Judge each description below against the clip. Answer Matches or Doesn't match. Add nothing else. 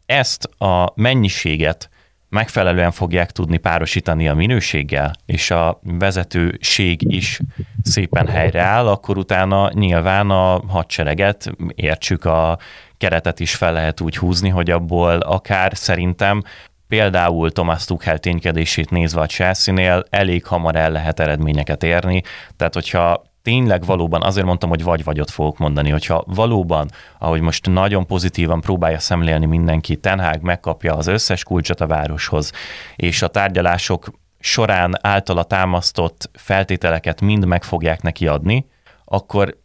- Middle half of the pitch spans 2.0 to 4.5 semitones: Matches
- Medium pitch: Doesn't match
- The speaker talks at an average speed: Matches